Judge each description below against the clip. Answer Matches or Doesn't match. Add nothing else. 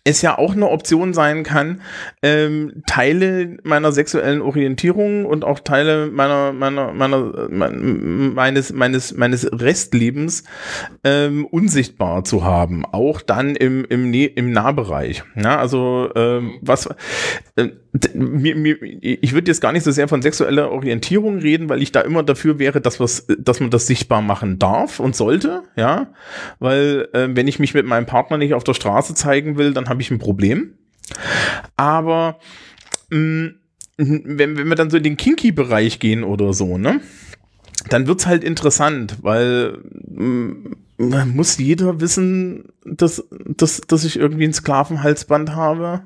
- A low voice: Doesn't match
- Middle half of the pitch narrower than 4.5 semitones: Matches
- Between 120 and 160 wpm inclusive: Matches